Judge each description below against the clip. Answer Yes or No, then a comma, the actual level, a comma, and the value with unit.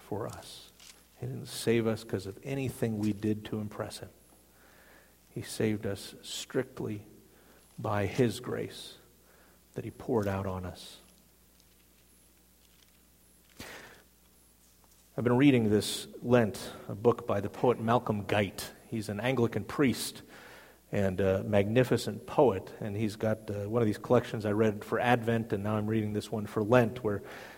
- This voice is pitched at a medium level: No, low, 105 Hz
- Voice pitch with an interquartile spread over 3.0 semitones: Yes, average, 3.4 semitones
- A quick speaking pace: No, average, 145 wpm